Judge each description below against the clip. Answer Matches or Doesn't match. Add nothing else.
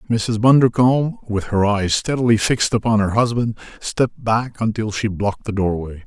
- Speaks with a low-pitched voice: Matches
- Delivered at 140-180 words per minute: Matches